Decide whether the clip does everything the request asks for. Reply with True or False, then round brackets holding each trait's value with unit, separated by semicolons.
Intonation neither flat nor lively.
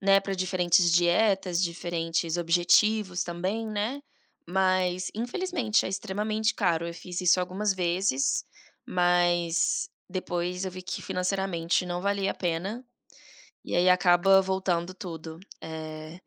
False (2.1 semitones)